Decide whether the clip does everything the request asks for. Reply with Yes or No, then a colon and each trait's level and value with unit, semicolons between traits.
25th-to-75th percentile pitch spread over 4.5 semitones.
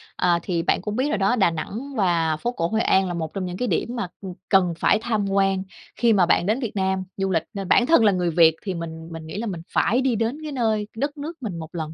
Yes: average, 5.0 semitones